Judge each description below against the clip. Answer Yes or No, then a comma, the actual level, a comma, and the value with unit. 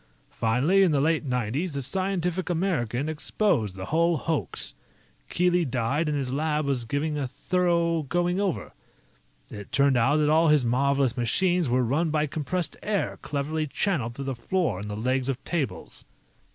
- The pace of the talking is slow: No, average, 165 wpm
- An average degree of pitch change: Yes, average, 5.0 semitones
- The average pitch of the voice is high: No, medium, 150 Hz